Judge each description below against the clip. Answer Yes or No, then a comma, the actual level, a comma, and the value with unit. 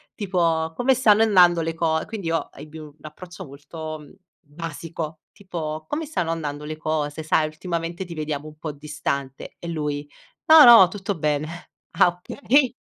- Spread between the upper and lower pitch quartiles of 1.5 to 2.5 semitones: No, average, 2.9 semitones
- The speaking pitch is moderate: Yes, medium, 160 Hz